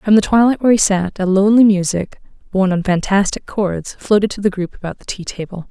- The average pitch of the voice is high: Yes, high, 195 Hz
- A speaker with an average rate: No, fast, 220 wpm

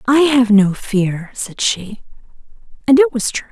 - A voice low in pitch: No, high, 235 Hz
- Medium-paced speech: Yes, average, 170 wpm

